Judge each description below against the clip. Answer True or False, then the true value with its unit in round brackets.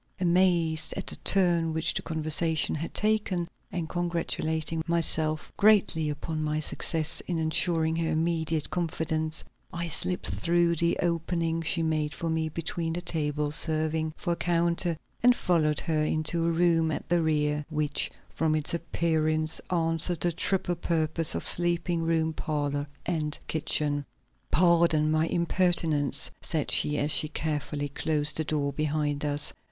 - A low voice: False (160 Hz)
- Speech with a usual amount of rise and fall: False (1.7 semitones)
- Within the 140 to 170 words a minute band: True (145 wpm)